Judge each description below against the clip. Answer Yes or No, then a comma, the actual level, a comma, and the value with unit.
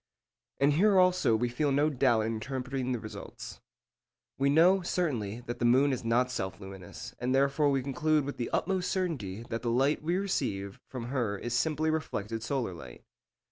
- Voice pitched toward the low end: Yes, low, 130 Hz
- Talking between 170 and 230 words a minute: Yes, average, 180 wpm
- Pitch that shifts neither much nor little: Yes, average, 4.7 semitones